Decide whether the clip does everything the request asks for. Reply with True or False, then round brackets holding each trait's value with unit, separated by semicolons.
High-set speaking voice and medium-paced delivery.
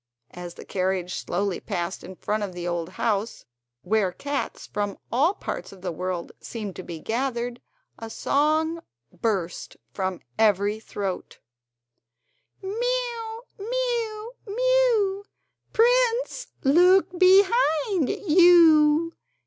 False (285 Hz; 110 wpm)